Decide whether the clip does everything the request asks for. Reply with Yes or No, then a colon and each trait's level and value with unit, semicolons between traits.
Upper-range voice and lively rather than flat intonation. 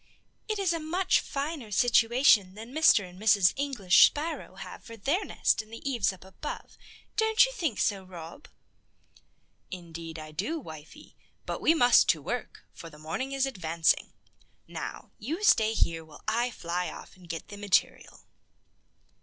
Yes: high, 220 Hz; wide, 8.0 semitones